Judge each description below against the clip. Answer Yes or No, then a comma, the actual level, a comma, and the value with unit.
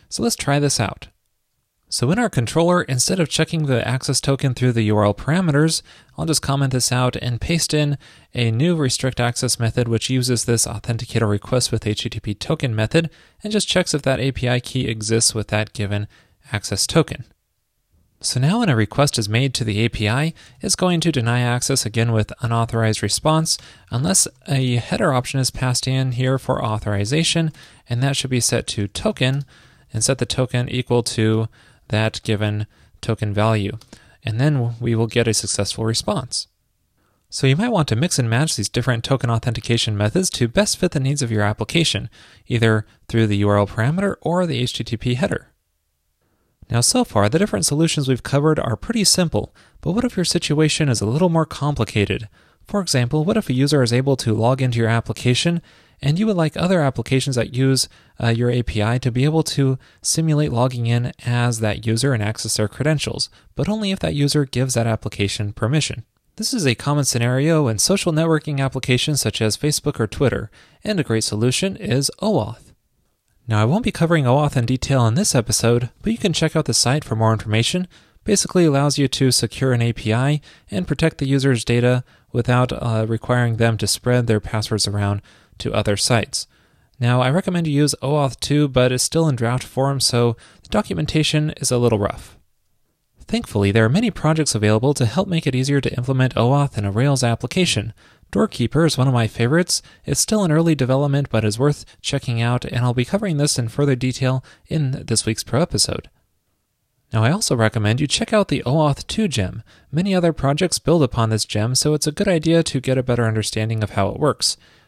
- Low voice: Yes, low, 125 Hz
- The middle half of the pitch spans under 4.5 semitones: No, average, 4.8 semitones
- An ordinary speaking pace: Yes, average, 195 wpm